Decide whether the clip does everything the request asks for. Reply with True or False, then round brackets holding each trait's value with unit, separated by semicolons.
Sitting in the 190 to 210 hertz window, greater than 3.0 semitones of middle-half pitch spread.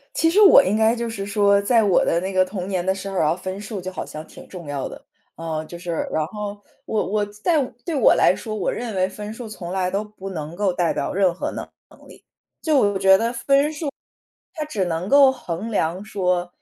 True (200 Hz; 3.5 semitones)